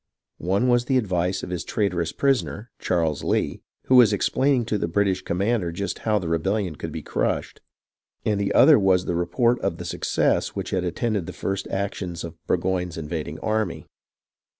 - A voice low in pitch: Yes, very low, 95 Hz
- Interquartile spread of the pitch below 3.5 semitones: No, average, 4.0 semitones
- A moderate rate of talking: Yes, average, 185 wpm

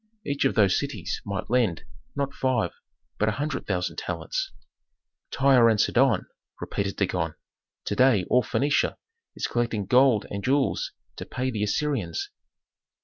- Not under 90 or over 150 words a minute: Yes, average, 145 wpm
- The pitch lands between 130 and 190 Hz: No, low, 120 Hz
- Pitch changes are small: No, average, 5.1 semitones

